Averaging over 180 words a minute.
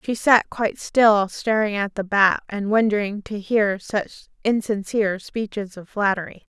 No: average, 155 wpm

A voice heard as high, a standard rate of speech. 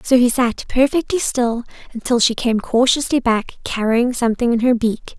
Yes: high, 240 Hz; average, 175 wpm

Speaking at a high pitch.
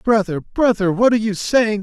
Yes: high, 210 Hz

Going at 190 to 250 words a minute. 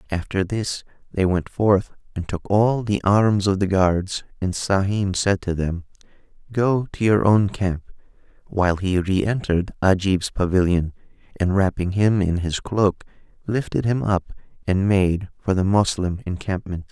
No: average, 155 wpm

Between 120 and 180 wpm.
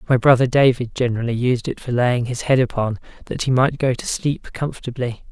No: fast, 205 wpm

